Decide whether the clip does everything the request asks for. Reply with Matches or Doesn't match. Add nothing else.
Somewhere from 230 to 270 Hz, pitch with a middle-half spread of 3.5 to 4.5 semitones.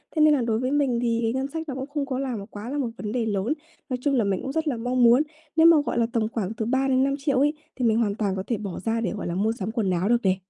Matches